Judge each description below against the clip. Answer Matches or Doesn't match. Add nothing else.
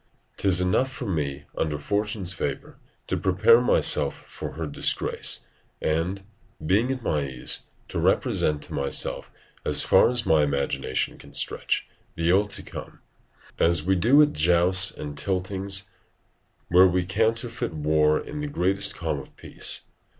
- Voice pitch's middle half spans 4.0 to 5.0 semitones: Matches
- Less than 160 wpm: Matches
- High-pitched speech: Doesn't match